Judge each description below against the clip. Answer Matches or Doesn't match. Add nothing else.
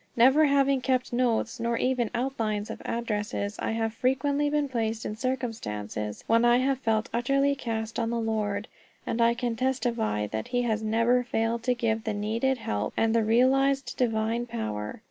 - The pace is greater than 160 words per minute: Matches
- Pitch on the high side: Matches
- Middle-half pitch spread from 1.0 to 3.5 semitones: Matches